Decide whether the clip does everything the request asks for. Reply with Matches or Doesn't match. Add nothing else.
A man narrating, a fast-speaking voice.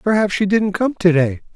Doesn't match